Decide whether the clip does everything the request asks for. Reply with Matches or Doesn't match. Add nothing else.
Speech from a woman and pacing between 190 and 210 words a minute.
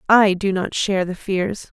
Matches